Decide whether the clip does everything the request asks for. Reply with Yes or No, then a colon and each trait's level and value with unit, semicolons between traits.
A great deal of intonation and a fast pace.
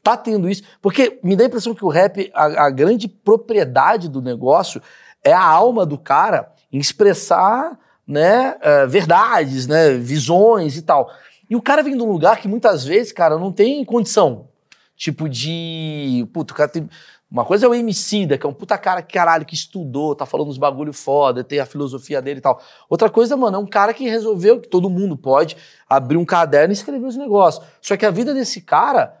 Yes: wide, 6.7 semitones; fast, 200 wpm